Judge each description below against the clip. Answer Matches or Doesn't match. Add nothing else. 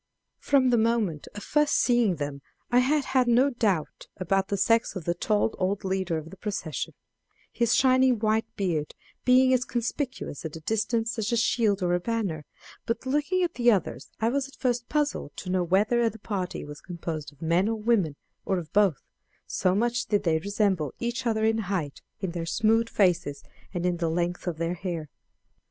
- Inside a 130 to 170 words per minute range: Doesn't match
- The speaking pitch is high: Matches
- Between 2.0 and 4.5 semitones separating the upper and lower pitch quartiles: Doesn't match